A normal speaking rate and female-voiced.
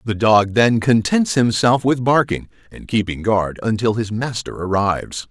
No: average, 160 wpm; male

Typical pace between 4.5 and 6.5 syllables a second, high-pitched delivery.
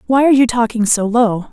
Yes: 5.9 syllables/s; high, 235 Hz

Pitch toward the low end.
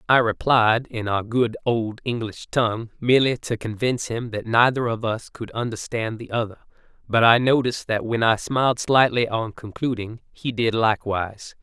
Yes: low, 115 Hz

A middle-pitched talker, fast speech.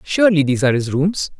Yes: medium, 155 Hz; fast, 215 wpm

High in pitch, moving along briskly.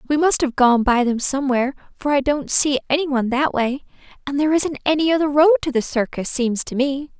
Yes: very high, 275 Hz; fast, 225 wpm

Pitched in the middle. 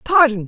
No: very high, 260 Hz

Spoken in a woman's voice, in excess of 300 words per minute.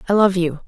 No: female; fast, 270 wpm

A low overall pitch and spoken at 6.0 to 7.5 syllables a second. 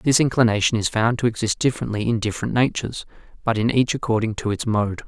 Yes: low, 115 Hz; 6.5 syllables/s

